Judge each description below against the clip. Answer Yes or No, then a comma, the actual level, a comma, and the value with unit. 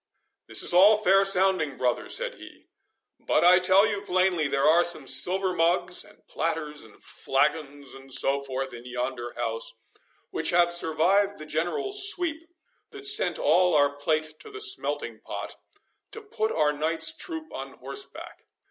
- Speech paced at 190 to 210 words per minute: No, average, 160 wpm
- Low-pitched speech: No, medium, 170 Hz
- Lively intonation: Yes, wide, 5.8 semitones